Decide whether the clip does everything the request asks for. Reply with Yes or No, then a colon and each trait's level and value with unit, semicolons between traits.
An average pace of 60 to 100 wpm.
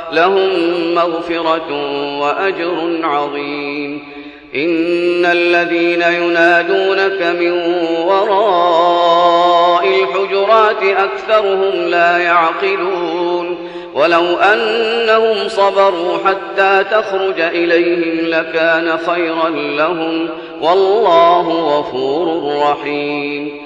Yes: slow, 65 wpm